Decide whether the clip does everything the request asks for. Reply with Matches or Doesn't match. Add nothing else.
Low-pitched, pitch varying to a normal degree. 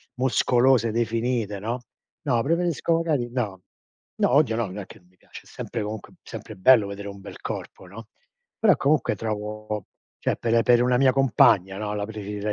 Matches